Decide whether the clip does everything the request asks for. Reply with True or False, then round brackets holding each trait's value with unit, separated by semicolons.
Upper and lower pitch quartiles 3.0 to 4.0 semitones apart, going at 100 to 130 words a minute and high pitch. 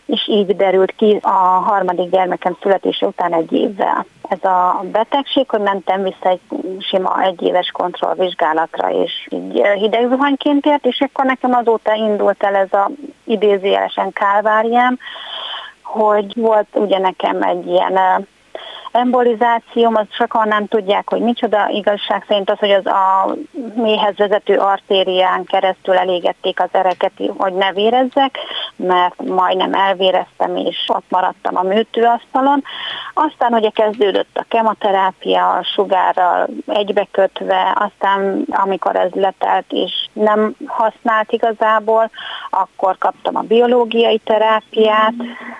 True (3.4 semitones; 120 wpm; 210 Hz)